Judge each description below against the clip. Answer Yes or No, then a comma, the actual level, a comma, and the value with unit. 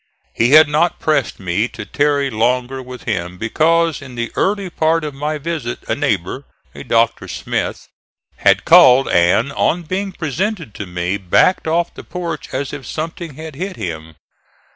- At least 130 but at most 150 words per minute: No, average, 165 wpm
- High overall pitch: No, medium, 140 Hz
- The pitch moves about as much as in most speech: No, wide, 6.1 semitones